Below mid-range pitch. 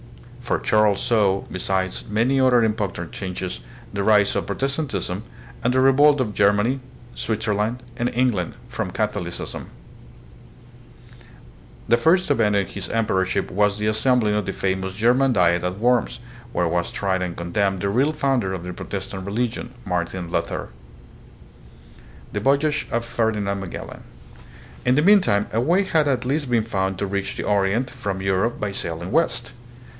Yes: low, 105 Hz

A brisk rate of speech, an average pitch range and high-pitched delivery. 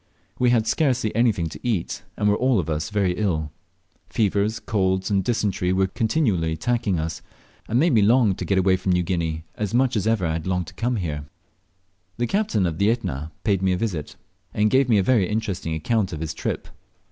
No: fast, 210 wpm; average, 4.5 semitones; low, 100 Hz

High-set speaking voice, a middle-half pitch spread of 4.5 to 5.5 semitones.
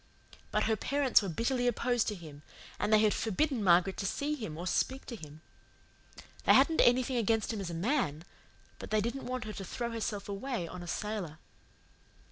Yes: high, 215 Hz; average, 5.1 semitones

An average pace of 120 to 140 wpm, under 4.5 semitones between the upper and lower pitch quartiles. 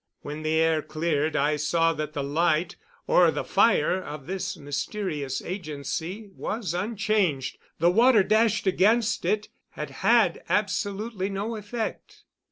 No: slow, 135 wpm; average, 5.3 semitones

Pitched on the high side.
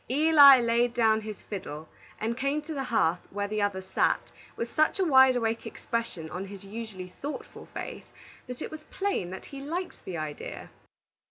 Yes: high, 230 Hz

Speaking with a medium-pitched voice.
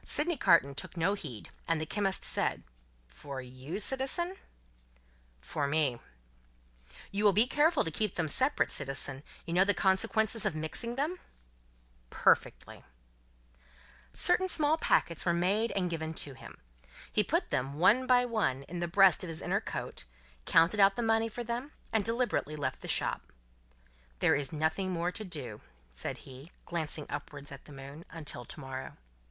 Yes: medium, 175 Hz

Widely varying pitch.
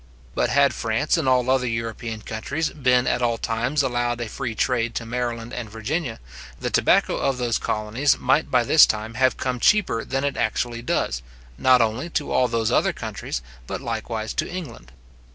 No: average, 2.7 semitones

